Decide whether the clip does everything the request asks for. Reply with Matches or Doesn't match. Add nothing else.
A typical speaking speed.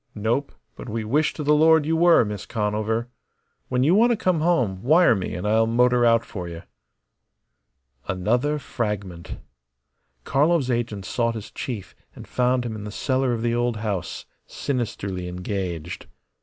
Matches